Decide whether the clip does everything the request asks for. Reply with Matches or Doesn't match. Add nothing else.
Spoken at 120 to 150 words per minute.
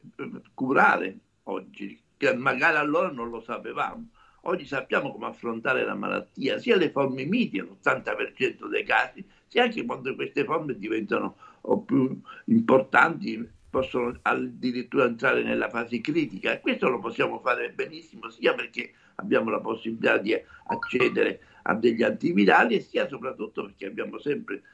Matches